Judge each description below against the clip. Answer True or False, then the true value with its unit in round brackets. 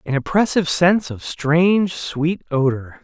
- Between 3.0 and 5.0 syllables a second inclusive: True (4.6 syllables/s)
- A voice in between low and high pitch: True (160 Hz)